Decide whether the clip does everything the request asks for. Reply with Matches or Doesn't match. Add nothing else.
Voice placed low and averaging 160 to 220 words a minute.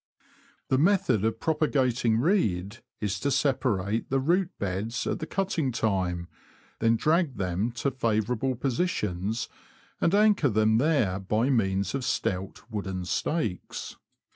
Doesn't match